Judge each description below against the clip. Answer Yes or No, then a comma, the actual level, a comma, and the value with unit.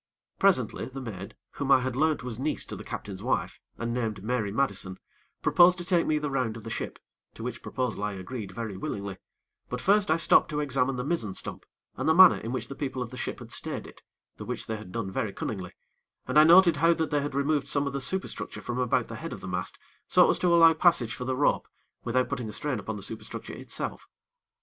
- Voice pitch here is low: Yes, low, 130 Hz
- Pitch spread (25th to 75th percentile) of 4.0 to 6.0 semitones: Yes, average, 5.2 semitones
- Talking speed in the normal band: No, fast, 235 wpm